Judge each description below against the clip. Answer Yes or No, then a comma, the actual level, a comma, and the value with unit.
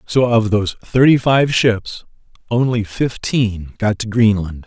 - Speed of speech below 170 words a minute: Yes, average, 140 wpm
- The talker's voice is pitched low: Yes, low, 110 Hz